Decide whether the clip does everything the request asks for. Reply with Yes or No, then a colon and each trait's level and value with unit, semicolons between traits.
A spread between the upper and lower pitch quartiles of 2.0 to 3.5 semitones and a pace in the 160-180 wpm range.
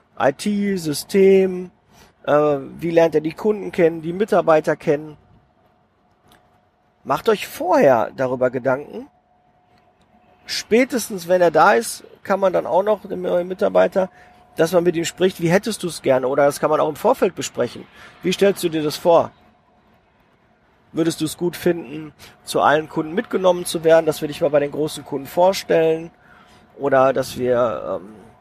No: average, 4.1 semitones; average, 165 wpm